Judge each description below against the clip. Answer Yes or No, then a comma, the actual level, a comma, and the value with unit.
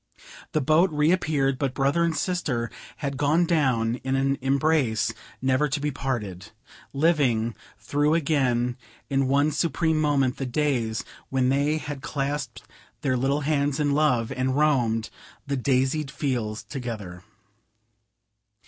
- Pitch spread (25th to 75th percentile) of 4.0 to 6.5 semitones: No, average, 3.0 semitones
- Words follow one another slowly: Yes, slow, 130 wpm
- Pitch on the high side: No, low, 135 Hz